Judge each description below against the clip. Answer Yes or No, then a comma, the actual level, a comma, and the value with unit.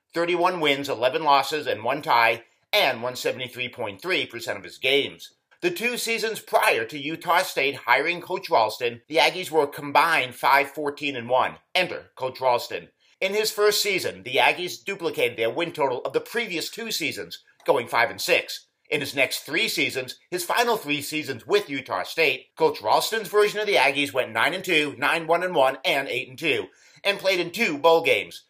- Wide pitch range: Yes, wide, 7.5 semitones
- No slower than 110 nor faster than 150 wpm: No, average, 160 wpm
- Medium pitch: Yes, medium, 170 Hz